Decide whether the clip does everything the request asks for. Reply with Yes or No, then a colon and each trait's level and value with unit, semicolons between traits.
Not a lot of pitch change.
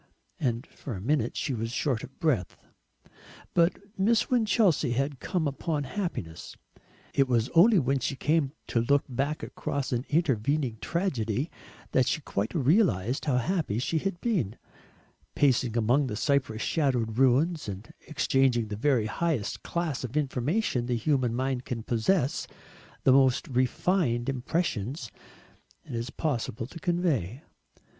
No: average, 5.0 semitones